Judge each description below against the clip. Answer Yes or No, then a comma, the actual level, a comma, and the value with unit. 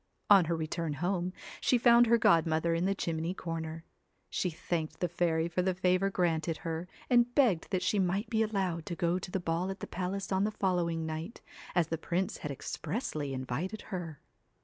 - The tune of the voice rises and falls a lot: No, average, 2.9 semitones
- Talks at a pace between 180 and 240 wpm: Yes, average, 195 wpm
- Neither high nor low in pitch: Yes, medium, 175 Hz